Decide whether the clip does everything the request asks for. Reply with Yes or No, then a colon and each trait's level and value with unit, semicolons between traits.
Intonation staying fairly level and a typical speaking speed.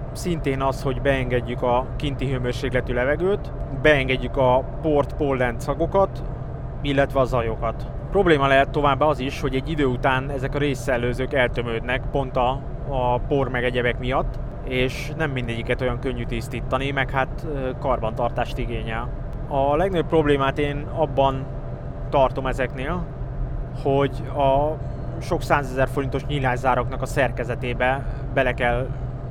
Yes: narrow, 1.8 semitones; average, 125 wpm